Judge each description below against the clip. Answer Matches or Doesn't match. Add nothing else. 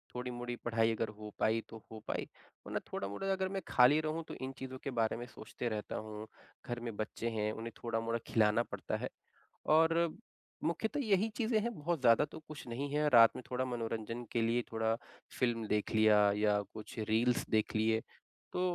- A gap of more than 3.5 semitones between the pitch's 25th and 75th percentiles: Matches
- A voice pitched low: Matches